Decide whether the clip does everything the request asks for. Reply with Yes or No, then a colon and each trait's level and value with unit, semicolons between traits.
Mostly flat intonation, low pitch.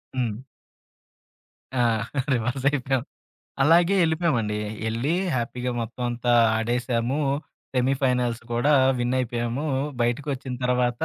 Yes: narrow, 2.3 semitones; low, 125 Hz